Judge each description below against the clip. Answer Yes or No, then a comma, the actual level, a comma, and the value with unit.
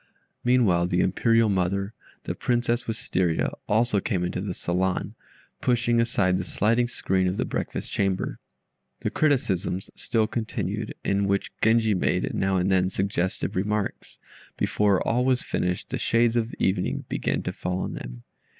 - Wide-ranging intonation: No, average, 3.9 semitones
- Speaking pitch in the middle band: No, low, 100 Hz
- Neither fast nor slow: Yes, average, 150 wpm